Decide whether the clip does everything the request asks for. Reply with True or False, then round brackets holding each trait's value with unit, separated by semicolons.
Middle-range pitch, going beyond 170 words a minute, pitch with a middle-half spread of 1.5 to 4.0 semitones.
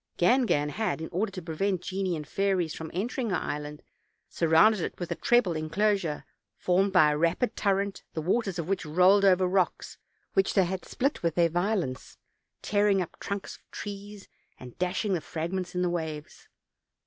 True (180 Hz; 180 wpm; 3.4 semitones)